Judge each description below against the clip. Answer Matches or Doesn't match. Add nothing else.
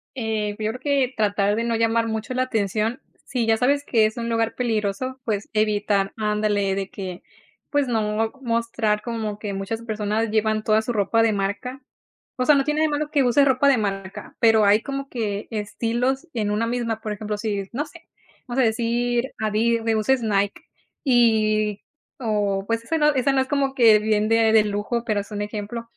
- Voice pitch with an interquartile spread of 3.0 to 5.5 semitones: Doesn't match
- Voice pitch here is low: Doesn't match